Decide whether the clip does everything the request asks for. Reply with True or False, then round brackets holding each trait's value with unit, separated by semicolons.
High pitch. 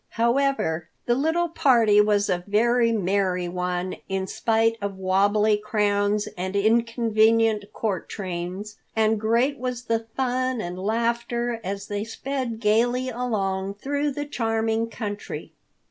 True (220 Hz)